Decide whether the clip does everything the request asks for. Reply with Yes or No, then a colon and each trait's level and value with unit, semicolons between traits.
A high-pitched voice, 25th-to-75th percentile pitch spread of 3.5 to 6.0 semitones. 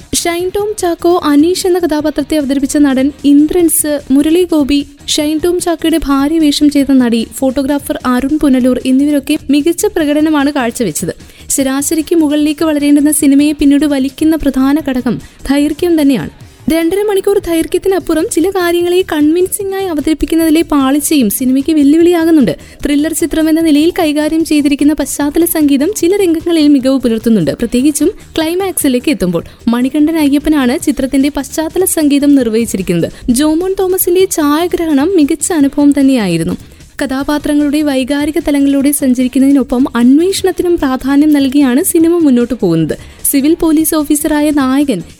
No: very high, 295 Hz; average, 3.0 semitones